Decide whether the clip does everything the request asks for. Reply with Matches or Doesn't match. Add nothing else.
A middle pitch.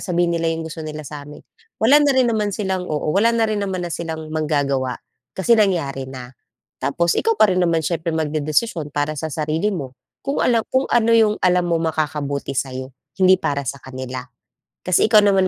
Matches